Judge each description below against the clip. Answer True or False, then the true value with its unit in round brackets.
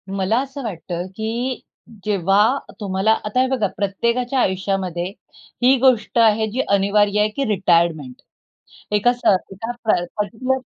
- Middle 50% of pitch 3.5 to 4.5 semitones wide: True (4.0 semitones)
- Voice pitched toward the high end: True (210 Hz)